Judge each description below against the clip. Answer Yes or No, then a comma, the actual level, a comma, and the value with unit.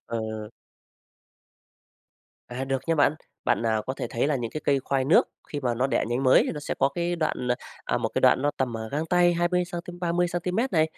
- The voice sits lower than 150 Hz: Yes, medium, 140 Hz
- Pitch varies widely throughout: Yes, wide, 5.8 semitones